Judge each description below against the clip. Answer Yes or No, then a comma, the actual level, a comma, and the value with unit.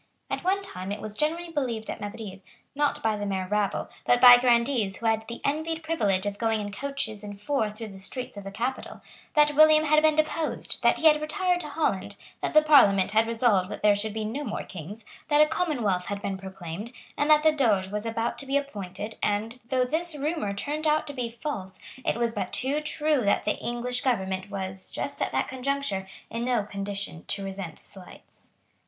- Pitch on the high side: Yes, high, 230 Hz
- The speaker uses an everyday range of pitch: No, wide, 6.4 semitones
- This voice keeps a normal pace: No, fast, 210 wpm